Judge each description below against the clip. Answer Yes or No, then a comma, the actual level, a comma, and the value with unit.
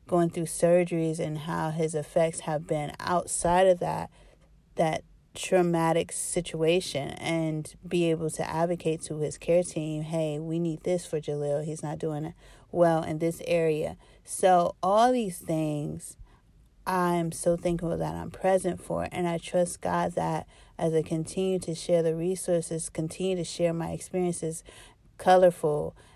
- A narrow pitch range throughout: Yes, narrow, 1.8 semitones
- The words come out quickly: No, average, 150 wpm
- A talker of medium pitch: Yes, medium, 165 Hz